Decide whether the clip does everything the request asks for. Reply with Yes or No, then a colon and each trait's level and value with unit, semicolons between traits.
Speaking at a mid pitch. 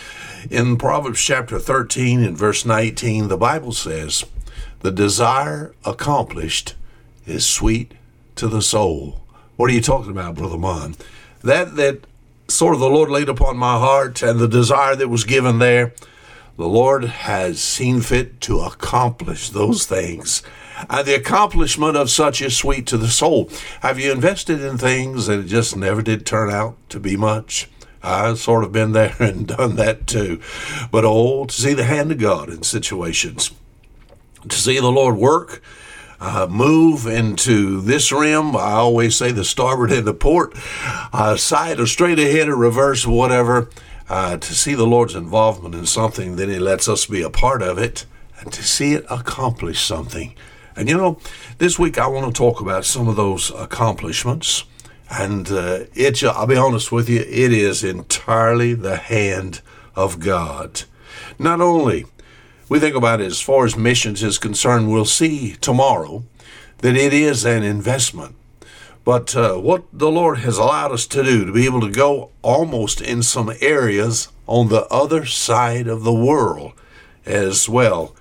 No: low, 120 Hz